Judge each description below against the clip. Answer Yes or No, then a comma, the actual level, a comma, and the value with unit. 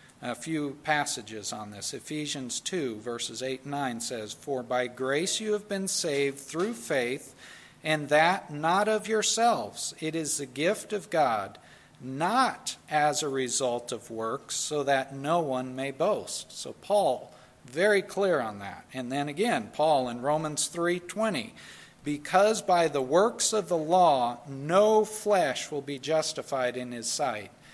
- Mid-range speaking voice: Yes, medium, 150 Hz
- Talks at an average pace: Yes, average, 155 wpm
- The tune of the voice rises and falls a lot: Yes, wide, 5.9 semitones